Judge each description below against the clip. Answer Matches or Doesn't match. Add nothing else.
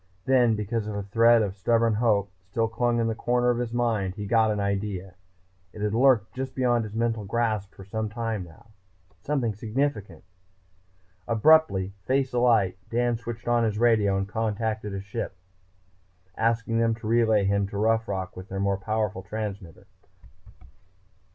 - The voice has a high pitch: Doesn't match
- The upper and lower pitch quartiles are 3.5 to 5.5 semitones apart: Doesn't match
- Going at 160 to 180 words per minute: Matches